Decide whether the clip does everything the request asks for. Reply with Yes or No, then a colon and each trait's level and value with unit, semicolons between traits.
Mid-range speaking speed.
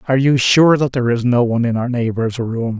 No: fast, 260 wpm